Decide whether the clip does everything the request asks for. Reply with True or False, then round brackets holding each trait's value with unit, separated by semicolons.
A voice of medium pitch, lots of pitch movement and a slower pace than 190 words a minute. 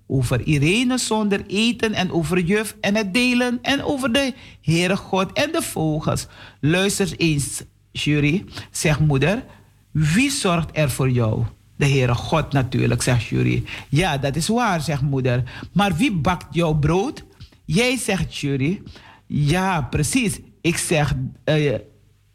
True (155 Hz; 7.2 semitones; 140 wpm)